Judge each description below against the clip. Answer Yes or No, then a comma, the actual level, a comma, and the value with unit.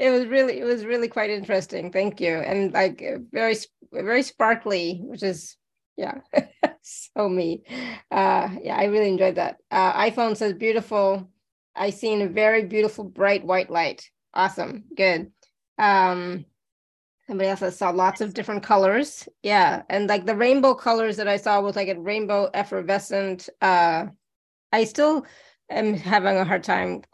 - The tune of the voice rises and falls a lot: No, average, 2.8 semitones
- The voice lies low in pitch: No, high, 205 Hz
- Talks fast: No, average, 155 wpm